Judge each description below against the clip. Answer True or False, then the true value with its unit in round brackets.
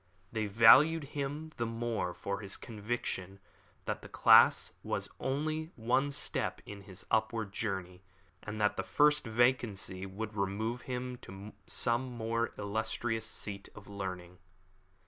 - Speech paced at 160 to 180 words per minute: False (135 wpm)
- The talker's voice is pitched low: True (110 Hz)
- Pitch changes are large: False (3.6 semitones)